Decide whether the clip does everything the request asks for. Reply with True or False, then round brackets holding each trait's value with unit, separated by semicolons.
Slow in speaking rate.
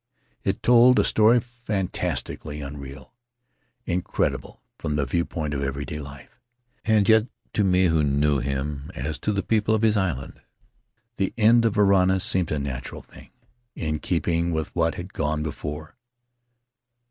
False (155 wpm)